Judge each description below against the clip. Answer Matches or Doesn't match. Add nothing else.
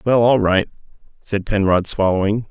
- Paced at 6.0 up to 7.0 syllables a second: Doesn't match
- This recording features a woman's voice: Doesn't match